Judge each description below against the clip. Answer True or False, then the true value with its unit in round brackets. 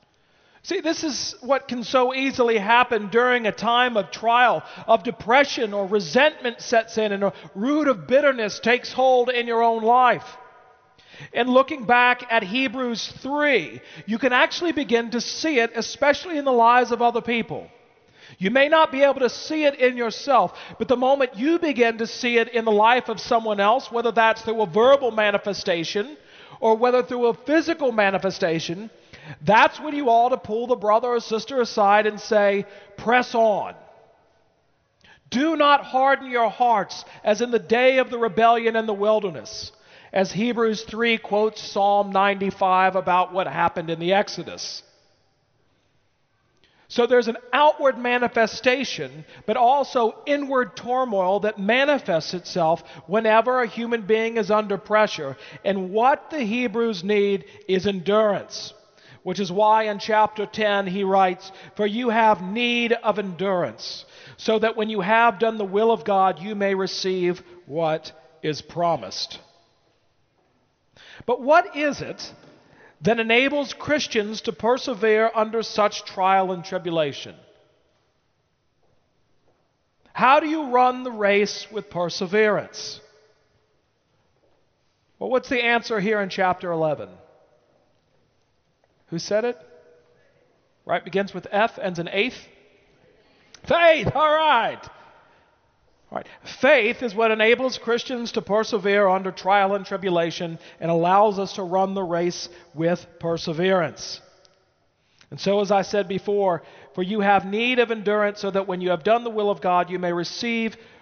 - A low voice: False (220 Hz)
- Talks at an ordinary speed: True (150 wpm)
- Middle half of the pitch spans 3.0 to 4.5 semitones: True (3.9 semitones)